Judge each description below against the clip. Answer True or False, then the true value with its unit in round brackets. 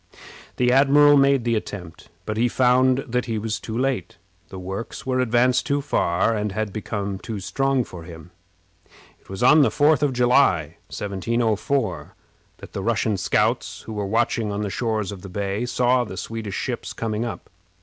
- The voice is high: False (115 Hz)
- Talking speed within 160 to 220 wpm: True (180 wpm)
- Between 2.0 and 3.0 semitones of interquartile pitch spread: False (4.0 semitones)